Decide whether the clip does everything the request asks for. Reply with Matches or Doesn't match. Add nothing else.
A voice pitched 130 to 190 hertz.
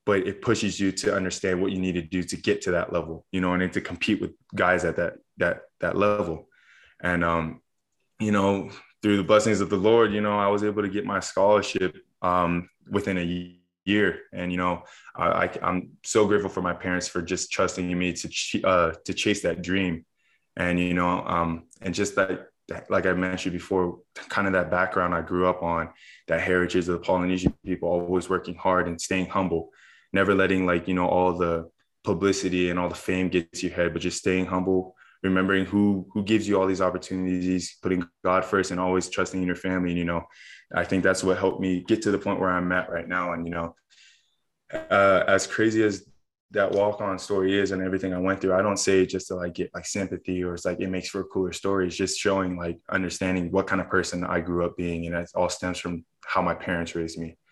Doesn't match